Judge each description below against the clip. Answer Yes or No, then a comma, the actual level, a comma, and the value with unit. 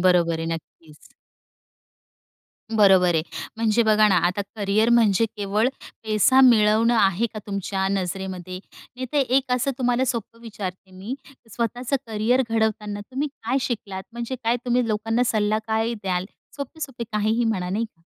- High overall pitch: Yes, high, 215 Hz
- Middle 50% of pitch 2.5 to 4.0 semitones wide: Yes, average, 3.6 semitones